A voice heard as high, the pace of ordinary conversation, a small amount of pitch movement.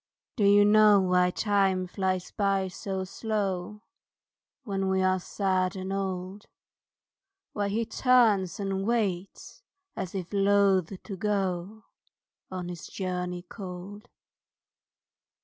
No: high, 195 Hz; slow, 115 wpm; narrow, 1.8 semitones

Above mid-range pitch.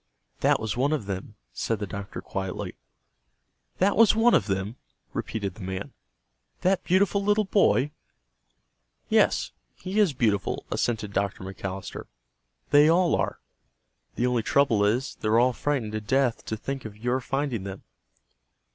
No: low, 115 Hz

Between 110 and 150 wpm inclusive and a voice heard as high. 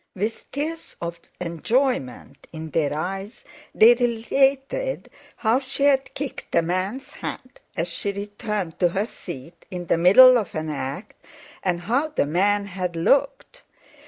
Yes: average, 145 wpm; high, 200 Hz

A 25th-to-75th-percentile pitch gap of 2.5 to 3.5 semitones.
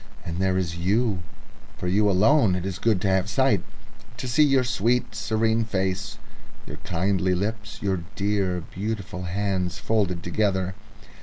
Yes: average, 3.1 semitones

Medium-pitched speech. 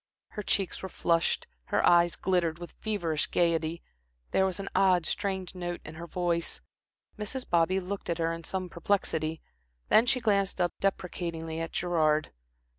Yes: medium, 175 Hz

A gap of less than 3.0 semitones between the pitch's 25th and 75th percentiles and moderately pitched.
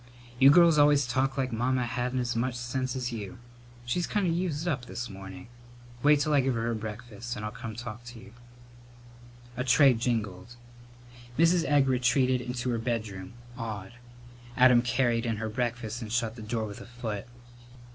No: narrow, 2.5 semitones; low, 120 Hz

